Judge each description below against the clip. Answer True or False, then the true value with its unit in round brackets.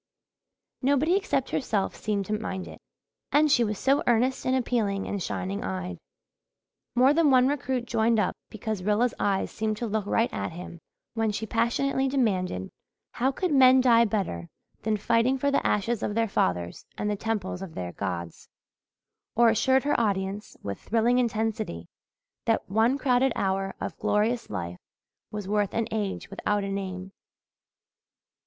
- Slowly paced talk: False (160 wpm)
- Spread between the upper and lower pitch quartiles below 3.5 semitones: False (4.1 semitones)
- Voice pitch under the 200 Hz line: False (220 Hz)